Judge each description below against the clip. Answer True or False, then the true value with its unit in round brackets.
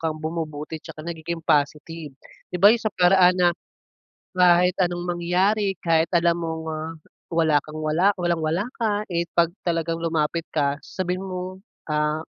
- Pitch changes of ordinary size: False (2.2 semitones)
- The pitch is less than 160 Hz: False (170 Hz)